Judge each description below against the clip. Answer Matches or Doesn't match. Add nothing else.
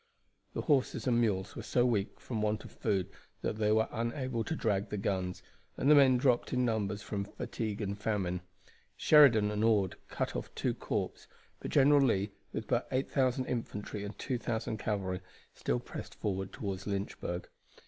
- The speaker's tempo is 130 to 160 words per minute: Doesn't match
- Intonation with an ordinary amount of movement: Matches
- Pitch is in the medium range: Doesn't match